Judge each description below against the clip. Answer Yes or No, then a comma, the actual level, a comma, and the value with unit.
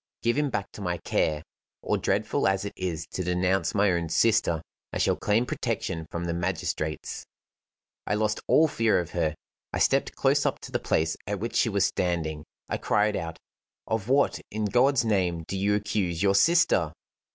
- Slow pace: No, average, 185 wpm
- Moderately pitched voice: No, very low, 95 Hz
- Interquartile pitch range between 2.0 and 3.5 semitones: No, average, 4.1 semitones